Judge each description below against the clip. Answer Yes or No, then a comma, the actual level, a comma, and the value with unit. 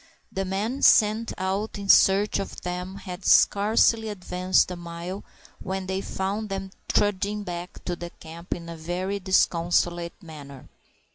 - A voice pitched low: No, high, 190 Hz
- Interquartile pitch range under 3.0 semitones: Yes, narrow, 2.5 semitones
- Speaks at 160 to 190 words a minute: No, average, 145 wpm